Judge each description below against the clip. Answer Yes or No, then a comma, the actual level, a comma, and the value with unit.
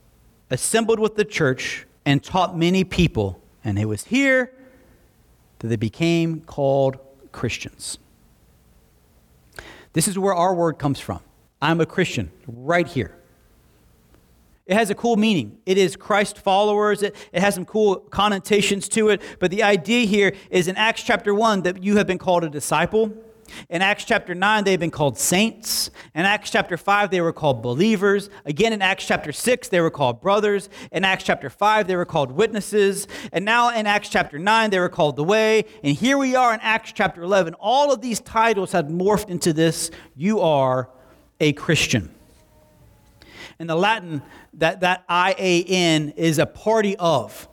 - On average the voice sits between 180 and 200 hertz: Yes, medium, 185 Hz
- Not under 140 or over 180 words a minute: Yes, average, 175 wpm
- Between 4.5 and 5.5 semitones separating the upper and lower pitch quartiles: Yes, average, 5.2 semitones